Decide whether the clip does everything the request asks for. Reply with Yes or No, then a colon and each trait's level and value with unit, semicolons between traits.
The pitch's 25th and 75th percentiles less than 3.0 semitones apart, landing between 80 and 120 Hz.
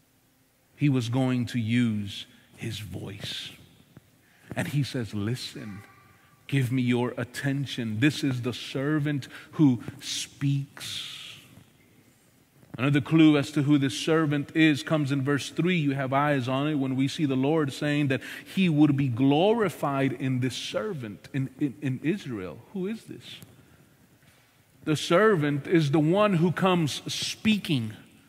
No: narrow, 2.5 semitones; medium, 140 Hz